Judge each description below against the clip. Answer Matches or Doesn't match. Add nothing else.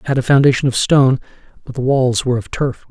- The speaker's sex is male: Matches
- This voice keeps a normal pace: Doesn't match